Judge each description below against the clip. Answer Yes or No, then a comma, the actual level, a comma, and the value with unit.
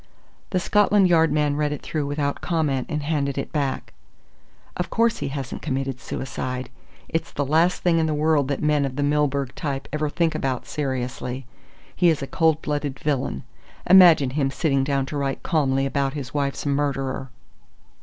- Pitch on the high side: No, medium, 145 Hz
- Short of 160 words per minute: No, average, 175 wpm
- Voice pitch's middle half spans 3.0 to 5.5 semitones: No, narrow, 2.4 semitones